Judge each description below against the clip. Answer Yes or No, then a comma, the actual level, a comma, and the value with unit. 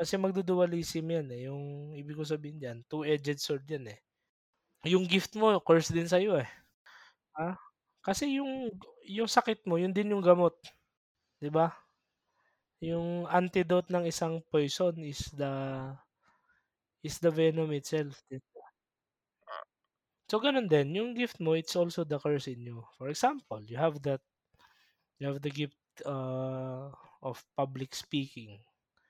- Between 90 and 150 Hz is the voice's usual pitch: No, medium, 160 Hz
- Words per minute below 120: No, average, 145 wpm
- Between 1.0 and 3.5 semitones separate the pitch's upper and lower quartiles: No, average, 4.4 semitones